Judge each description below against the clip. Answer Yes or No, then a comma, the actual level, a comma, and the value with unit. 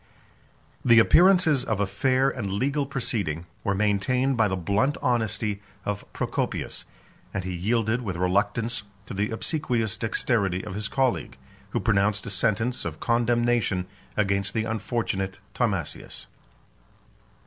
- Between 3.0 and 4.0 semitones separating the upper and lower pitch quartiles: Yes, average, 3.6 semitones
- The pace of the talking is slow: Yes, slow, 130 wpm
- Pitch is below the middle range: Yes, low, 110 Hz